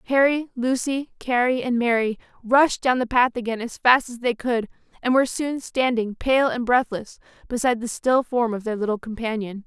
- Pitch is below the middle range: No, high, 240 Hz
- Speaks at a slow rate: No, average, 185 wpm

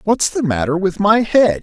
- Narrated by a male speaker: Yes, male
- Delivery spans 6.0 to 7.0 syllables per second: No, 4.6 syllables/s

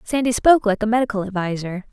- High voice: Yes, high, 215 Hz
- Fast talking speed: No, average, 190 wpm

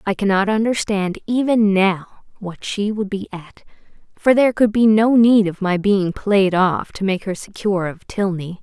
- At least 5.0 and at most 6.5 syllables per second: No, 4.5 syllables/s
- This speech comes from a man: No, female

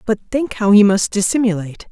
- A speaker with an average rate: Yes, average, 190 wpm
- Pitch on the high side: Yes, high, 210 Hz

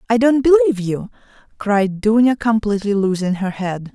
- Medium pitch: No, high, 215 Hz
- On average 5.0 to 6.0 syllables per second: Yes, 5.2 syllables/s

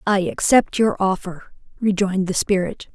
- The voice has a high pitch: Yes, high, 195 Hz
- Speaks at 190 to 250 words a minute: No, average, 145 wpm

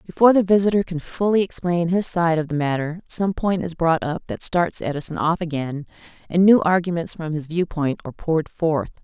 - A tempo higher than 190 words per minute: Yes, average, 200 wpm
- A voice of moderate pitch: Yes, medium, 170 Hz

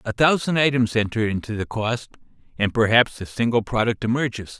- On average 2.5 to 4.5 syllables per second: No, 5.4 syllables/s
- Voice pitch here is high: No, low, 115 Hz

